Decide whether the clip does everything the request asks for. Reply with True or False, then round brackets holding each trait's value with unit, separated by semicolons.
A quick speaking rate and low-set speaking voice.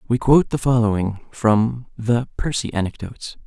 False (140 wpm; 115 Hz)